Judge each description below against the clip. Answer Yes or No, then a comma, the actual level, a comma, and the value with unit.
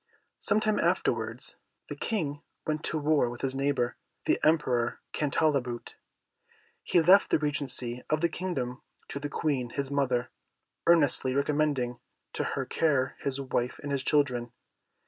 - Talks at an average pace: Yes, average, 145 wpm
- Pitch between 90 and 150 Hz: Yes, medium, 140 Hz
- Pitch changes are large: No, average, 3.5 semitones